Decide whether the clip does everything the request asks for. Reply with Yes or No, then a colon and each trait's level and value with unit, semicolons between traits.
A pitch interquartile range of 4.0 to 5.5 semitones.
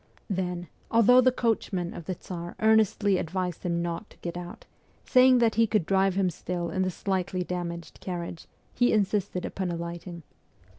No: average, 3.3 semitones